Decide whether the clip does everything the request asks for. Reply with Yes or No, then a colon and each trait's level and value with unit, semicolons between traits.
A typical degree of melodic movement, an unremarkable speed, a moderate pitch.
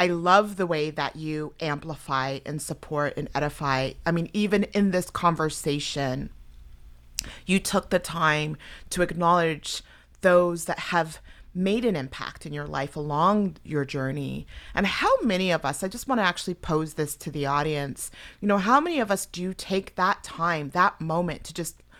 Yes: average, 4.1 semitones; average, 175 wpm; medium, 160 Hz